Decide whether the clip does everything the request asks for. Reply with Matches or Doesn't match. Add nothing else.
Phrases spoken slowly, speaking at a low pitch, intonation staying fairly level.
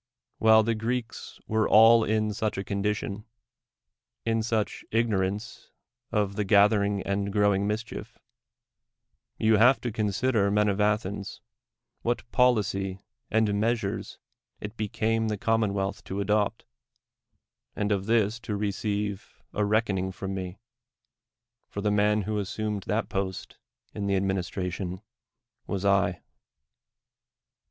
Matches